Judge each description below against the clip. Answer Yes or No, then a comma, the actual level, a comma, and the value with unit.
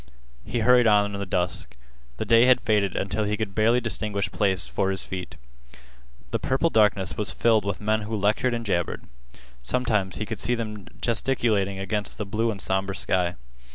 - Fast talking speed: No, average, 185 wpm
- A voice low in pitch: Yes, low, 105 Hz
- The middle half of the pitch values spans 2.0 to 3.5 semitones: Yes, narrow, 2.6 semitones